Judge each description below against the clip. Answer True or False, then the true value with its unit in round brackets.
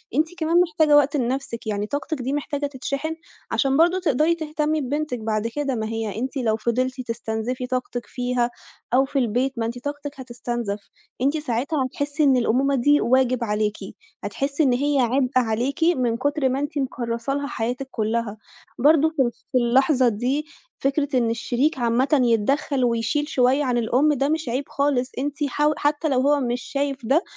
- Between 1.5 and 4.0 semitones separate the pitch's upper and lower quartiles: True (3.4 semitones)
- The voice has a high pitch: True (265 Hz)